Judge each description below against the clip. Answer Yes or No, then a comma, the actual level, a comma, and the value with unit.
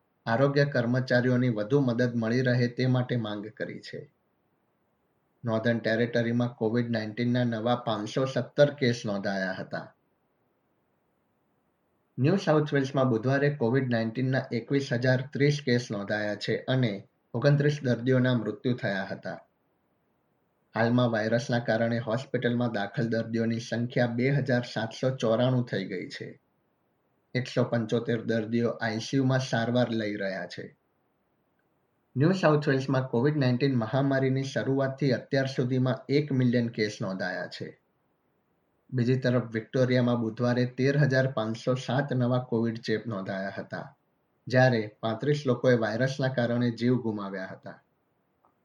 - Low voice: Yes, low, 120 Hz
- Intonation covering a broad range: No, narrow, 2.4 semitones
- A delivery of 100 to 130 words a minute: Yes, average, 120 wpm